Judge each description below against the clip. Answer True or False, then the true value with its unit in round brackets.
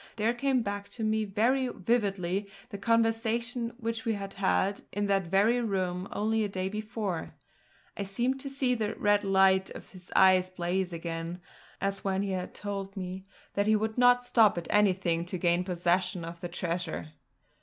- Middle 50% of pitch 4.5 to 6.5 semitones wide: False (3.3 semitones)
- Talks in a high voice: True (200 Hz)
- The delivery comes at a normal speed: True (175 wpm)